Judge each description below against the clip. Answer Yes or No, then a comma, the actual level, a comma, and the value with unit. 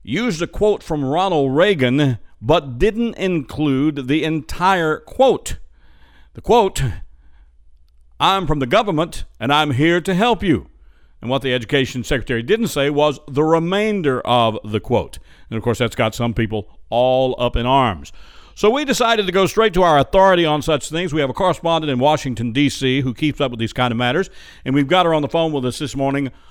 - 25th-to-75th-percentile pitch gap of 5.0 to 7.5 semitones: Yes, wide, 5.5 semitones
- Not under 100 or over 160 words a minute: No, average, 195 wpm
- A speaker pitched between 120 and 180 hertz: Yes, medium, 140 Hz